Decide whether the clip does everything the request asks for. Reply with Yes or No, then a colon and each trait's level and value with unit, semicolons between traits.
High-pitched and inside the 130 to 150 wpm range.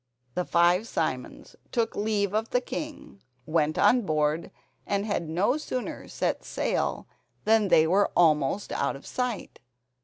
Yes: high, 200 Hz; average, 145 wpm